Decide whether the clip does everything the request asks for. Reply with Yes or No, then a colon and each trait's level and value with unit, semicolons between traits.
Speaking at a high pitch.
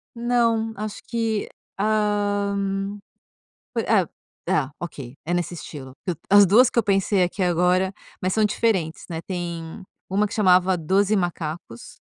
Yes: high, 195 Hz